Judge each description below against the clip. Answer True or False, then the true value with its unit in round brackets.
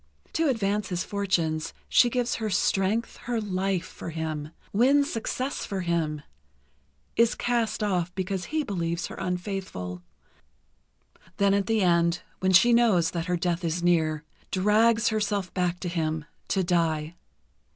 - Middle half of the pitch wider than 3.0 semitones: True (4.1 semitones)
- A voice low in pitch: False (185 Hz)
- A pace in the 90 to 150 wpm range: True (145 wpm)